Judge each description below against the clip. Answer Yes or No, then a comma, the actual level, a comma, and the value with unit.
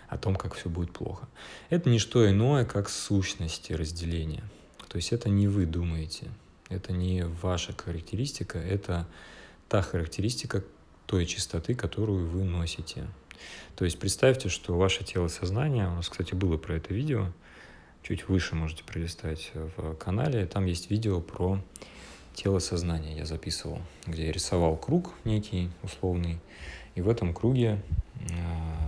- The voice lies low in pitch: Yes, very low, 90 Hz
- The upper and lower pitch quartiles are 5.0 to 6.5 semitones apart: No, average, 3.2 semitones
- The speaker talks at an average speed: Yes, average, 145 wpm